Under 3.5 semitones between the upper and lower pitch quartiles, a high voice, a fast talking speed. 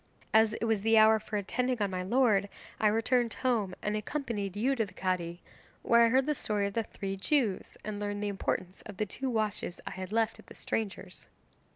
Yes: narrow, 2.6 semitones; high, 215 Hz; fast, 215 wpm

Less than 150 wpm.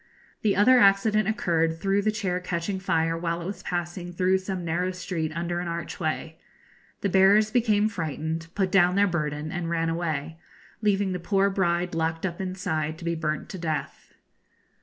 No: average, 175 wpm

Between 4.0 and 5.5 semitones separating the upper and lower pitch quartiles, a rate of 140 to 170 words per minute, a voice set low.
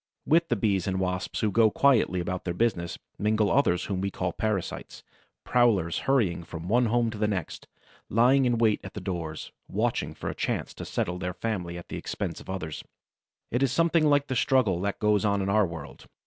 No: average, 4.8 semitones; fast, 205 wpm; low, 105 Hz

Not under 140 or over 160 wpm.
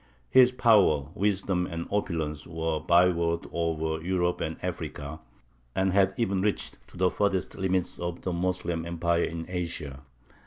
Yes: average, 150 wpm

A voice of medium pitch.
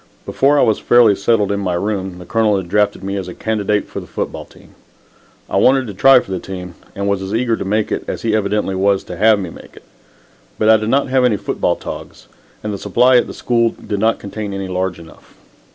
No: low, 105 Hz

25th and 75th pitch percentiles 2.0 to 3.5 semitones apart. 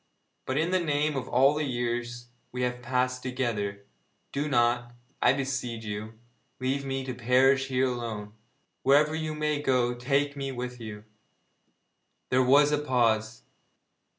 Yes: narrow, 2.5 semitones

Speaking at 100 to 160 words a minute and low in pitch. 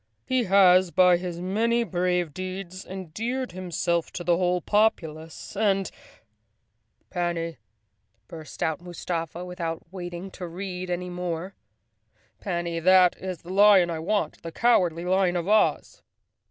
No: average, 140 wpm; medium, 180 Hz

